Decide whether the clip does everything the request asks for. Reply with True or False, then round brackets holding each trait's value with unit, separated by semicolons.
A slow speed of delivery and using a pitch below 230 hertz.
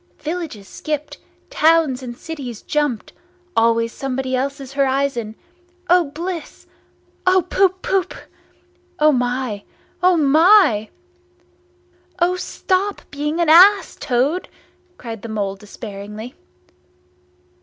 False (95 wpm; 285 Hz)